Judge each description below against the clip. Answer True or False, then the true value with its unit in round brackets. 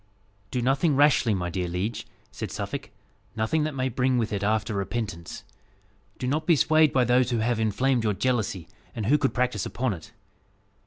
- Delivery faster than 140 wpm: True (180 wpm)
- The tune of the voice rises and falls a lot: False (4.0 semitones)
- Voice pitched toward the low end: True (120 Hz)